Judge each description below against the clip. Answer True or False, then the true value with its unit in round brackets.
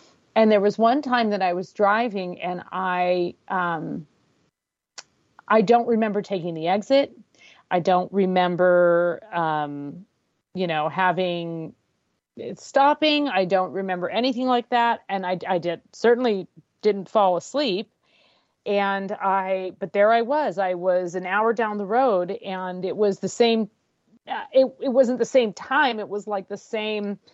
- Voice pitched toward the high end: True (200 Hz)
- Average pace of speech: True (155 wpm)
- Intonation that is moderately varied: True (4.1 semitones)